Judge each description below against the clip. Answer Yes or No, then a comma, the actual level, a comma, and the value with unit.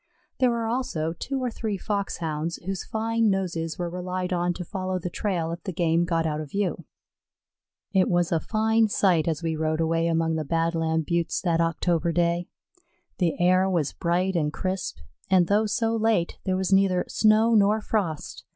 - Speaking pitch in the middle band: Yes, medium, 180 Hz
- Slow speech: No, average, 180 wpm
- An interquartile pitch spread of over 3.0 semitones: Yes, average, 3.5 semitones